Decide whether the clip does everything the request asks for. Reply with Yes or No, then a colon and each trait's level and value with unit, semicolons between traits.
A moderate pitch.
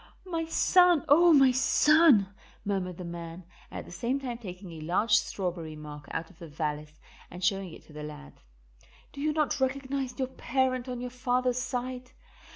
No: high, 240 Hz